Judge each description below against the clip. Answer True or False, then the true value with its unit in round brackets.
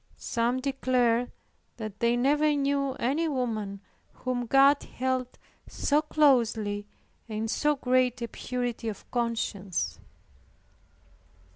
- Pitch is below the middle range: False (250 Hz)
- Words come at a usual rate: False (110 wpm)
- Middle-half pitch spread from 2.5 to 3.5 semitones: True (3.2 semitones)